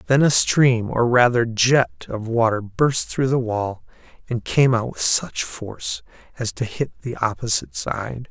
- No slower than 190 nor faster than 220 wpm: No, average, 175 wpm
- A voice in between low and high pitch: No, low, 115 Hz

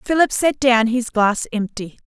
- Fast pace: No, average, 175 wpm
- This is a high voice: Yes, high, 240 Hz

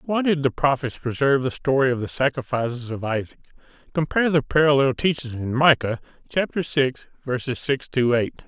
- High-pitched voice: No, low, 135 Hz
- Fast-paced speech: No, average, 170 wpm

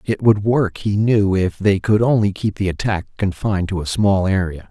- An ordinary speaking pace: No, fast, 215 wpm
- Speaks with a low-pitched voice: Yes, low, 100 Hz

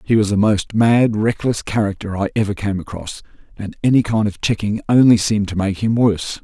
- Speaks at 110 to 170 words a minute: No, fast, 205 wpm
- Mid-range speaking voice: No, low, 105 Hz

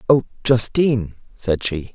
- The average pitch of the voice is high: No, low, 110 Hz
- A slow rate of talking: Yes, slow, 125 wpm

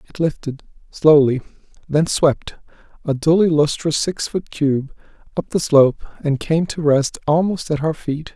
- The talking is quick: No, average, 160 wpm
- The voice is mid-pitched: Yes, medium, 150 Hz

